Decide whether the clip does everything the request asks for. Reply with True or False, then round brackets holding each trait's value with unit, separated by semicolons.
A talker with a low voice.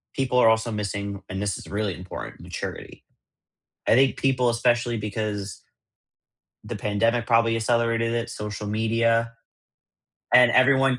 True (115 Hz)